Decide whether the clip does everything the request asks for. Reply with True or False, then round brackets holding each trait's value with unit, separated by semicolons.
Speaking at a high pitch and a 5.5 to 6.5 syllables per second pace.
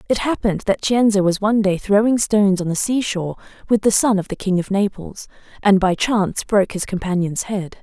True (200 Hz; 5.8 syllables/s)